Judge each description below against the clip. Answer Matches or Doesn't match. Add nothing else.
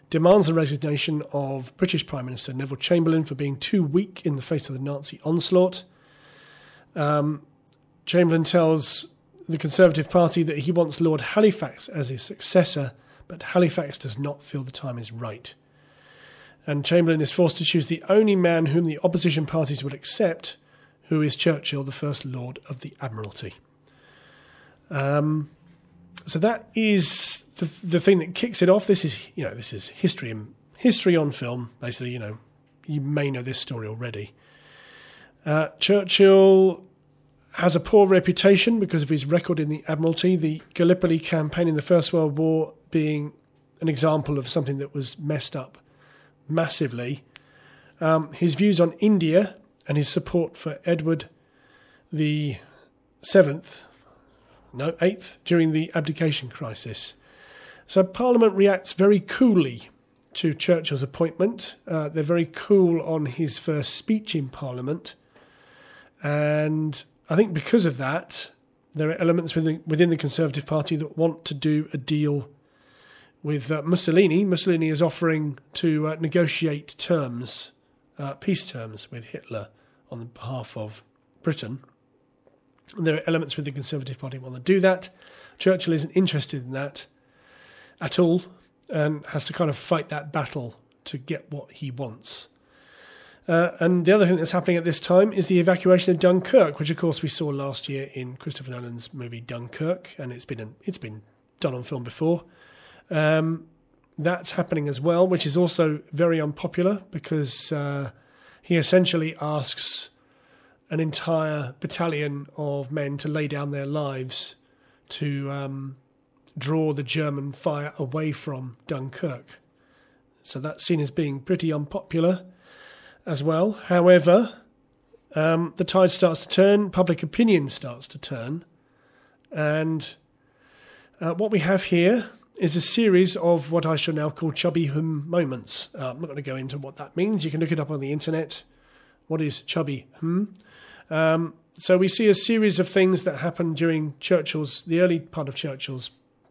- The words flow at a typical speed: Matches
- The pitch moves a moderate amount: Matches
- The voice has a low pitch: Doesn't match